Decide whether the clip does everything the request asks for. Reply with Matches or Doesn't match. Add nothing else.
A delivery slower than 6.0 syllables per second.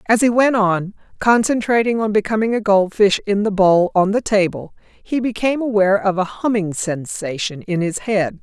Matches